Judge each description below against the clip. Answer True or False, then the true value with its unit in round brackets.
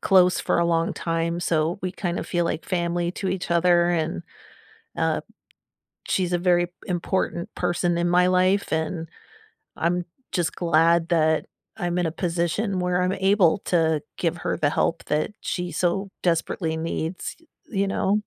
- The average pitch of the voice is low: False (175 Hz)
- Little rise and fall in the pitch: True (1.5 semitones)